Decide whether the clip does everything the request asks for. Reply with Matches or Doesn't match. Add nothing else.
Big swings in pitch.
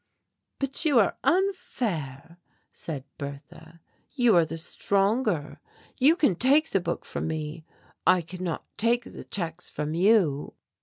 Matches